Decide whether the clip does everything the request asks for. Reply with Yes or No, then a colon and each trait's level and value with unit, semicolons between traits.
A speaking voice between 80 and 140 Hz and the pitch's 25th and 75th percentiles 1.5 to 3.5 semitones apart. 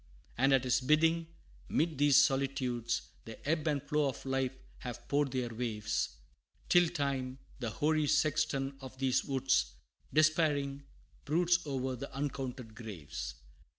Yes: low, 135 Hz; average, 2.8 semitones